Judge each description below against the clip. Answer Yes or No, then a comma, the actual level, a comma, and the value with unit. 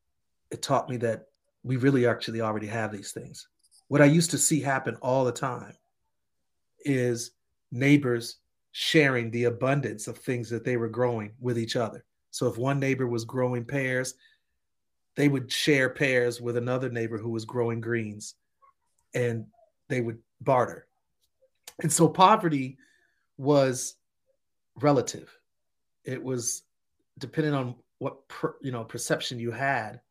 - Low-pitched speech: Yes, low, 125 Hz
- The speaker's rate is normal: Yes, average, 145 wpm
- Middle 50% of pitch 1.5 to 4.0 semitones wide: Yes, average, 3.0 semitones